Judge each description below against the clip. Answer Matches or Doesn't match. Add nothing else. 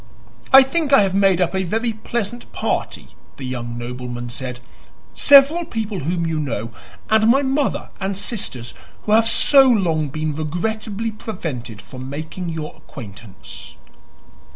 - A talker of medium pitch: Matches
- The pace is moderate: Matches